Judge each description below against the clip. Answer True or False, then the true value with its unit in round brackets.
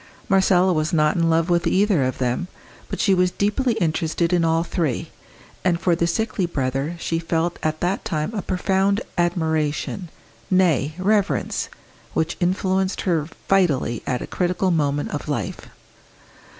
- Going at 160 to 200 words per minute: False (150 wpm)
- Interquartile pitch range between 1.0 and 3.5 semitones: True (3.1 semitones)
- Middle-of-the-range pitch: True (175 Hz)